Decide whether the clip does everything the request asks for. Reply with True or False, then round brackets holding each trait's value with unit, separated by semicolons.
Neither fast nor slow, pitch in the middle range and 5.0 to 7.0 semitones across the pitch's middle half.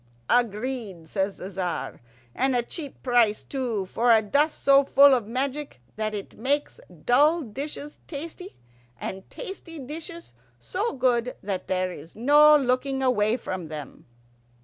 False (145 wpm; 250 Hz; 5.6 semitones)